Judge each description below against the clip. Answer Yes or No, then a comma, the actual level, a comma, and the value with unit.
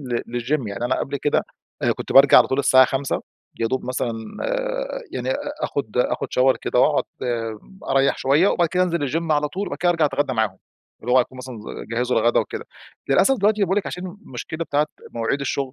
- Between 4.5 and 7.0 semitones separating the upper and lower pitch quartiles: Yes, average, 4.9 semitones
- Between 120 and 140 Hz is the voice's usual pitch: Yes, low, 135 Hz